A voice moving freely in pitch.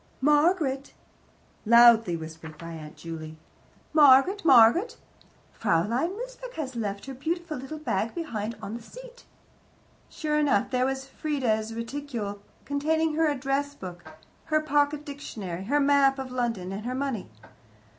Yes: wide, 5.9 semitones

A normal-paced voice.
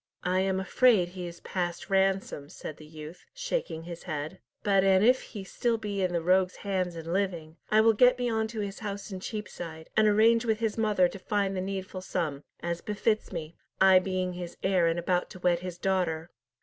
No: fast, 210 wpm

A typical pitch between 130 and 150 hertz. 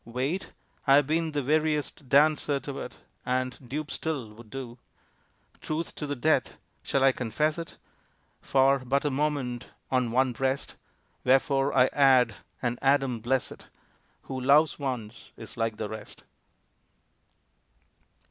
Yes: low, 135 Hz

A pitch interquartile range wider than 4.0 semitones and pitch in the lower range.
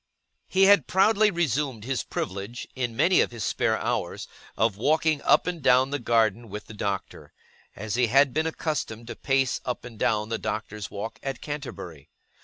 Yes: average, 5.3 semitones; low, 125 Hz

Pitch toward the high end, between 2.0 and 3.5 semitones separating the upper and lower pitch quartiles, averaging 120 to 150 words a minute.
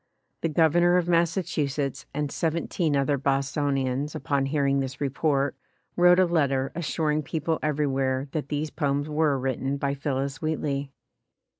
No: medium, 145 Hz; narrow, 2.5 semitones; average, 145 wpm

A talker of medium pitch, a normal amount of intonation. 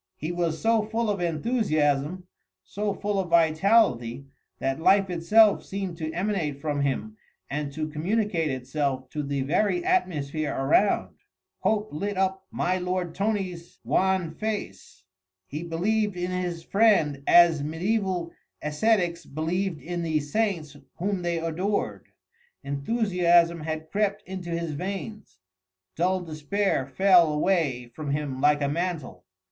Yes: medium, 170 Hz; average, 4.6 semitones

